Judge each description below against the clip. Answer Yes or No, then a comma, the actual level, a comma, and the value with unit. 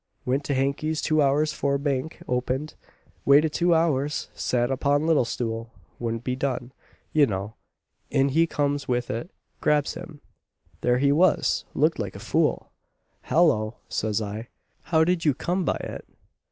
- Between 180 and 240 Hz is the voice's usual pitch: No, medium, 140 Hz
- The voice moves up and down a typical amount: Yes, average, 3.9 semitones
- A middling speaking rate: Yes, average, 155 wpm